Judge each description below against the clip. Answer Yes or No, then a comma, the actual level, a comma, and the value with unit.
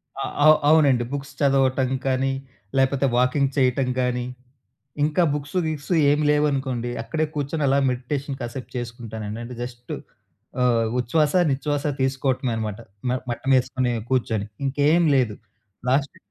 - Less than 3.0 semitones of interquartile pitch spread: Yes, narrow, 2.5 semitones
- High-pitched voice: No, low, 130 Hz